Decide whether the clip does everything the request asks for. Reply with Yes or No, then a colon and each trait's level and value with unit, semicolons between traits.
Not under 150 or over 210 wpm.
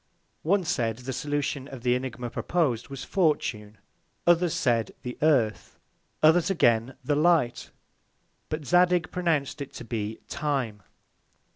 No: slow, 135 wpm